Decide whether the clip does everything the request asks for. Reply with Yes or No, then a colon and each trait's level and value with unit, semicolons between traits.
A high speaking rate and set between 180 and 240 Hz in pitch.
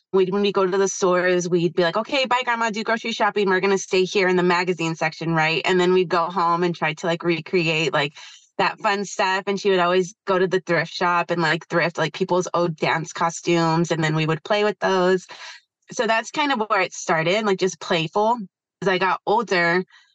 Yes: fast, 230 wpm; medium, 185 Hz